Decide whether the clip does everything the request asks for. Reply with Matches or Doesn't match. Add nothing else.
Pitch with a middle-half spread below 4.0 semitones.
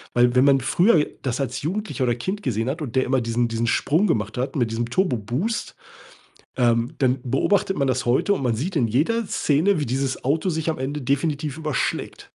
Doesn't match